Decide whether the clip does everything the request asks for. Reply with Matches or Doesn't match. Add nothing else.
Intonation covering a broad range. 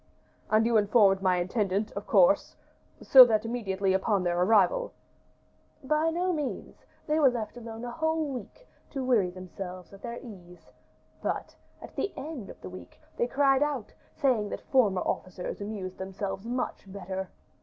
Matches